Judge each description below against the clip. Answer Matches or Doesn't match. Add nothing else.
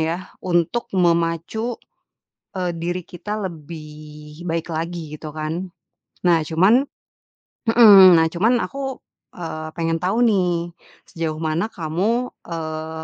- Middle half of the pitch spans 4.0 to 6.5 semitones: Doesn't match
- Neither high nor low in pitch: Matches